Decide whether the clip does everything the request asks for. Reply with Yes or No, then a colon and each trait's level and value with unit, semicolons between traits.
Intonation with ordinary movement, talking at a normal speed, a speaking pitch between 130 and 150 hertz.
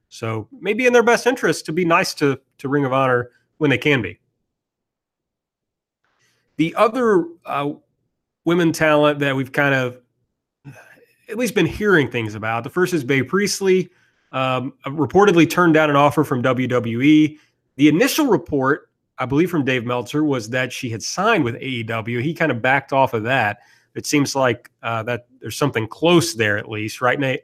Yes: average, 4.6 semitones; average, 175 wpm; medium, 140 Hz